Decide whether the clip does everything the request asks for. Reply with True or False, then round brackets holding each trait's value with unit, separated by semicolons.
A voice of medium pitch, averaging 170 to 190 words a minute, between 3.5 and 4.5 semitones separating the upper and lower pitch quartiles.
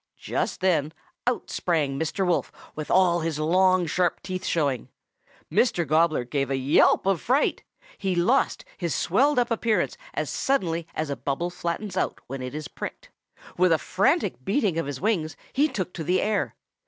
True (175 Hz; 175 wpm; 4.1 semitones)